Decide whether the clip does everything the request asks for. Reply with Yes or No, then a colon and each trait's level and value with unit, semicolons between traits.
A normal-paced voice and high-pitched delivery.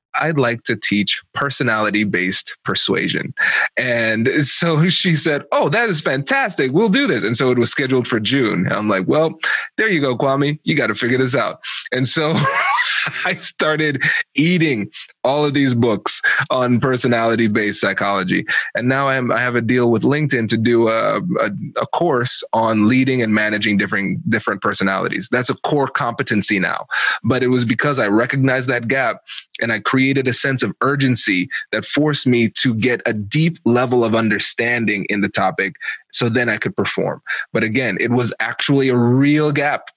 No: average, 180 wpm; low, 125 Hz